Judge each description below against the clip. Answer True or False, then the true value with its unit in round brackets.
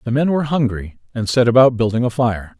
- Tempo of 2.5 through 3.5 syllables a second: False (6.0 syllables/s)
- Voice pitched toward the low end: True (120 Hz)